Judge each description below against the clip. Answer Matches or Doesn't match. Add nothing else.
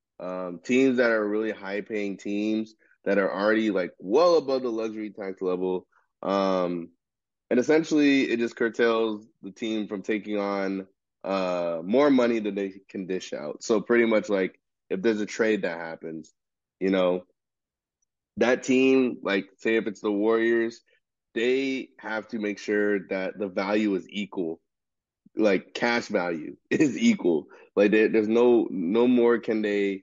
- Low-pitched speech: Matches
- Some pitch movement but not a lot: Matches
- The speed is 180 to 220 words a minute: Doesn't match